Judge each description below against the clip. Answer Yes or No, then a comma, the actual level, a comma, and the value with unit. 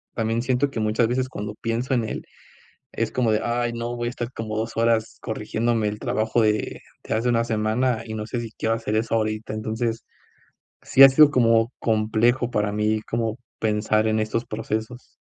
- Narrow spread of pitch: Yes, narrow, 1.6 semitones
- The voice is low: Yes, low, 115 Hz